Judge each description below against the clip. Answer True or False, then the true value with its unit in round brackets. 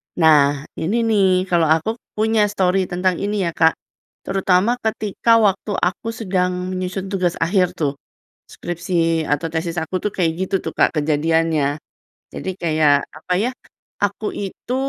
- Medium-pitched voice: True (180 Hz)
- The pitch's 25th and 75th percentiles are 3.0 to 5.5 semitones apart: True (3.3 semitones)